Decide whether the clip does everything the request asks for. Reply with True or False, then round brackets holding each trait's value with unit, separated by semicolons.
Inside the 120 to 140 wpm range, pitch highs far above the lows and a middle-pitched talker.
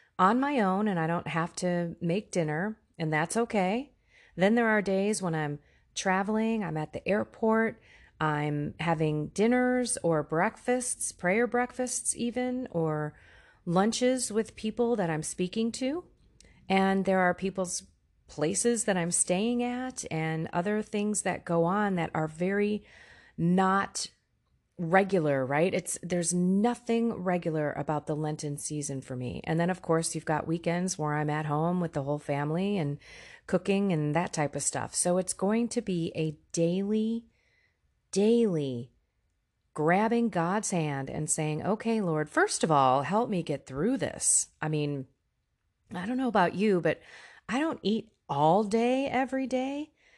False (155 wpm; 6.1 semitones; 180 Hz)